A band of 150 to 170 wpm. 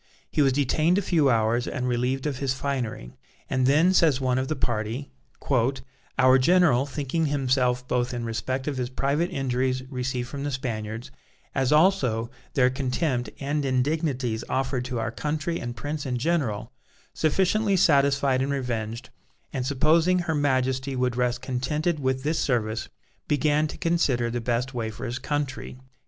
Yes: average, 160 wpm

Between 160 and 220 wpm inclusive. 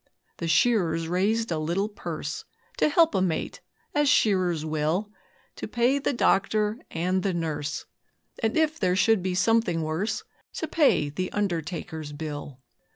No: average, 150 wpm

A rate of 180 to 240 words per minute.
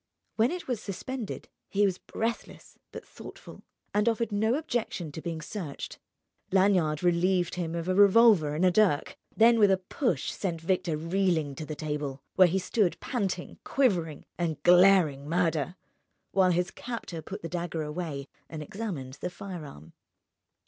No: average, 155 wpm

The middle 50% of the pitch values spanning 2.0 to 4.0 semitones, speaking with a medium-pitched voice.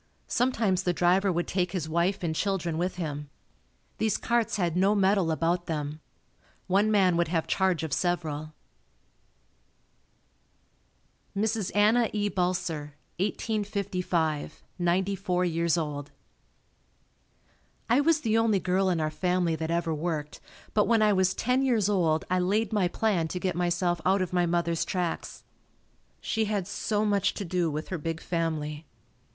Yes: average, 3.5 semitones; medium, 180 Hz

